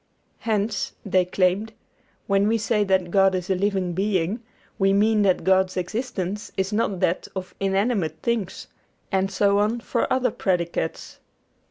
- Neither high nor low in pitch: No, high, 195 Hz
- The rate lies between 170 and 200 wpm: No, average, 150 wpm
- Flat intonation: Yes, narrow, 2.1 semitones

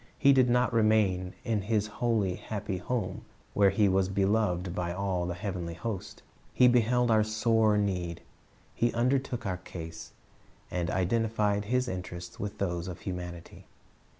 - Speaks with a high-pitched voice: No, low, 100 Hz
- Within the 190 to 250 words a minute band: No, average, 150 wpm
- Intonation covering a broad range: No, average, 3.9 semitones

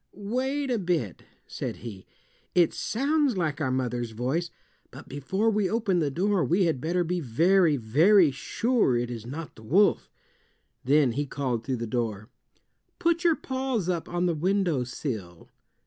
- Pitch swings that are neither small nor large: No, wide, 8.1 semitones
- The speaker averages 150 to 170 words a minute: Yes, average, 160 wpm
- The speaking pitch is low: No, medium, 165 Hz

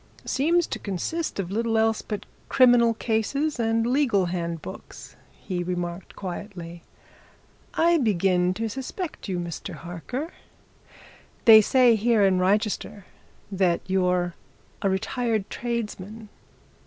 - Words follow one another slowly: Yes, slow, 115 wpm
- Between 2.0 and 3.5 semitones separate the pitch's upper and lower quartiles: No, average, 4.6 semitones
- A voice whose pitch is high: Yes, high, 210 Hz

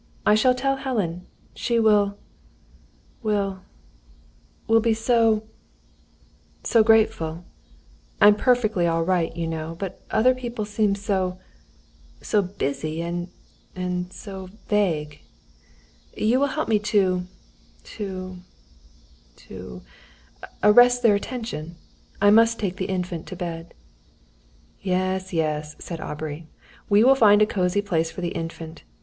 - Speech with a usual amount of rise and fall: Yes, average, 4.2 semitones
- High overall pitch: Yes, high, 195 Hz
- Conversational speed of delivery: No, slow, 120 wpm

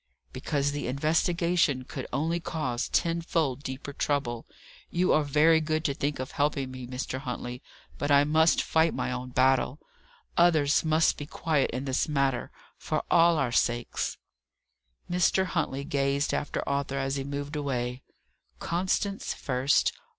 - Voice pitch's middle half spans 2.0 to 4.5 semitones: Yes, average, 3.4 semitones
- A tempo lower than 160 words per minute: Yes, average, 145 wpm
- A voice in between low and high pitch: Yes, medium, 145 Hz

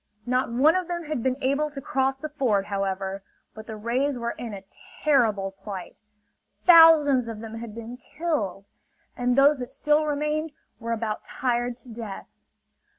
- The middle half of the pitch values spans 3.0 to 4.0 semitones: No, average, 5.0 semitones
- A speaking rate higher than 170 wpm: No, average, 165 wpm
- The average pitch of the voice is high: Yes, high, 245 Hz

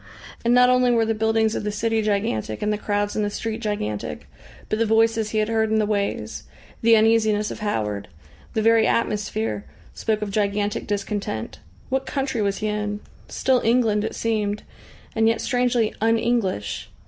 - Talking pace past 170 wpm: Yes, average, 180 wpm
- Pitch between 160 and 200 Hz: No, high, 215 Hz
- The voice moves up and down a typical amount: No, narrow, 1.7 semitones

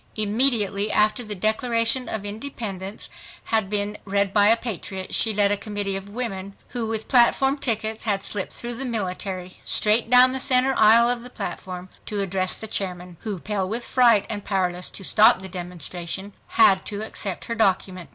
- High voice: Yes, high, 210 Hz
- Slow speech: No, average, 180 wpm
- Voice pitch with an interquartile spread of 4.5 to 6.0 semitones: No, average, 3.1 semitones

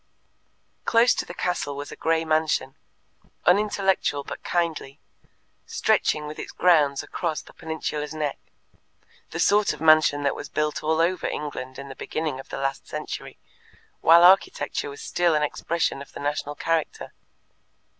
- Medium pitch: Yes, medium, 155 Hz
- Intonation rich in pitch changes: No, average, 3.2 semitones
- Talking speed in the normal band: Yes, average, 155 wpm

